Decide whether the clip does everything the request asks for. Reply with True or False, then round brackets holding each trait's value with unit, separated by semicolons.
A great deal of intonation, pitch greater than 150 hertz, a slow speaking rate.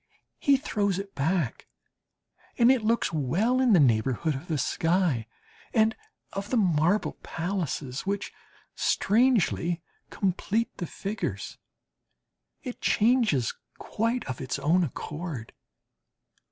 True (6.5 semitones; 185 Hz; 115 wpm)